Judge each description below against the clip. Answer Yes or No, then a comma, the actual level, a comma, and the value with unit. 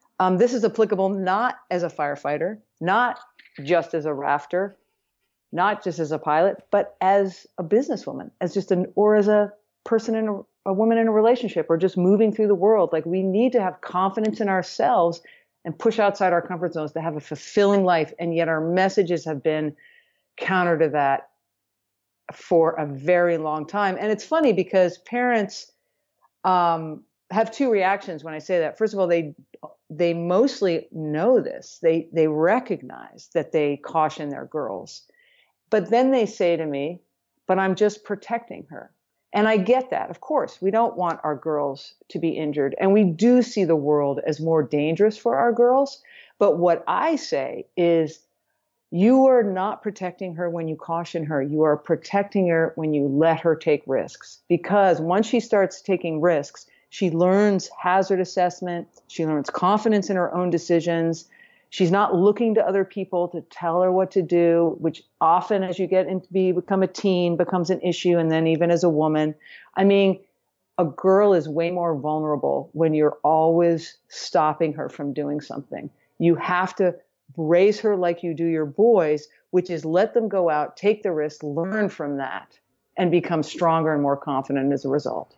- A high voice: No, medium, 180 Hz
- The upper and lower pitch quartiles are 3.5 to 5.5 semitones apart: Yes, average, 3.9 semitones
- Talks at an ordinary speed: Yes, average, 185 wpm